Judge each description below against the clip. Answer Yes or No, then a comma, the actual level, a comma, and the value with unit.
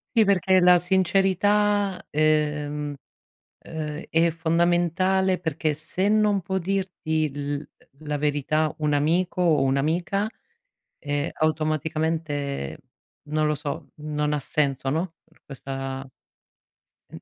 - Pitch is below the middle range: No, medium, 155 Hz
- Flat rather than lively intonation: No, average, 3.7 semitones